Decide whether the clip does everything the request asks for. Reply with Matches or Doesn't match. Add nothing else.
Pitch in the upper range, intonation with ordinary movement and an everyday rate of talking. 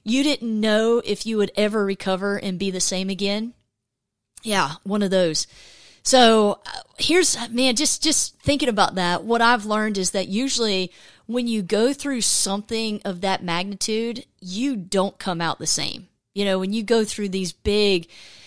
Matches